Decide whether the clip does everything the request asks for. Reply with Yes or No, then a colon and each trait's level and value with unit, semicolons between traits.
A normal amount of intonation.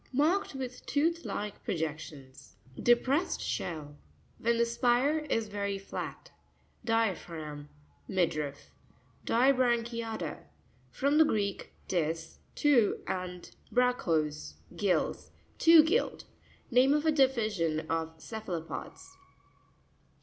No: wide, 8.1 semitones